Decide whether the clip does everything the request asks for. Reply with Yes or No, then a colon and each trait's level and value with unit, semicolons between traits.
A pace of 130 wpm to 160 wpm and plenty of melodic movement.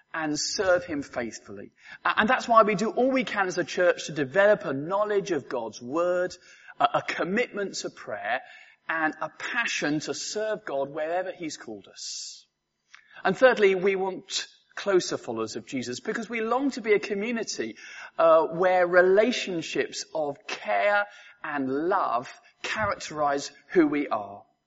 Yes: average, 155 wpm; wide, 6.8 semitones